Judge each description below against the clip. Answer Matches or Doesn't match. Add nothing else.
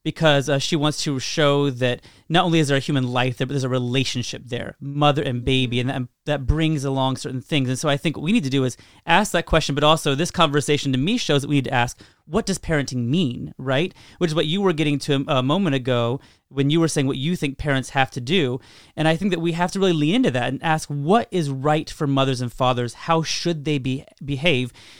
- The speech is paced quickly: Matches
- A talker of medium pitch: Matches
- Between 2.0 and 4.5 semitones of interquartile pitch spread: Matches